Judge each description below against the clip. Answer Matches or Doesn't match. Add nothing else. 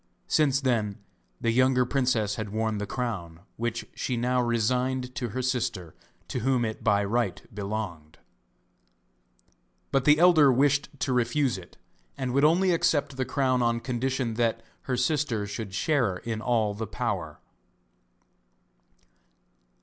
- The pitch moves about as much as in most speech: Matches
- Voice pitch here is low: Matches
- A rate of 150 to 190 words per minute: Doesn't match